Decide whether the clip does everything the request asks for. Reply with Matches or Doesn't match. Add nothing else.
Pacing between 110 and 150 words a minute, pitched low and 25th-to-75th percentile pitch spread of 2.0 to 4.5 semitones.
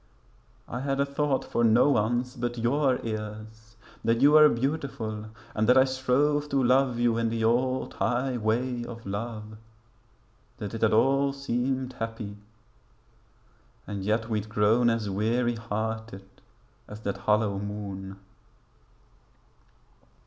Matches